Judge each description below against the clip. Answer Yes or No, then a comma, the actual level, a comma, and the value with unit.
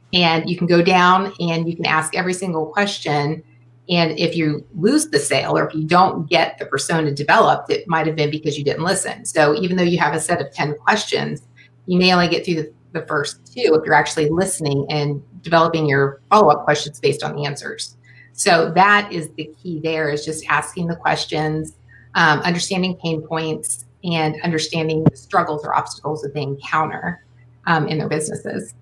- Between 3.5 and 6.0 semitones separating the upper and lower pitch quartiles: No, average, 2.9 semitones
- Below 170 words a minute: No, average, 195 wpm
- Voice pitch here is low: No, medium, 155 Hz